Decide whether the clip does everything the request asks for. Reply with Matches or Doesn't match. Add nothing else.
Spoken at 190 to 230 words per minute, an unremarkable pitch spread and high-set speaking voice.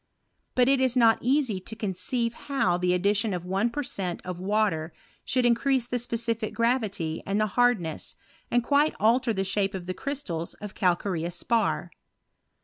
Doesn't match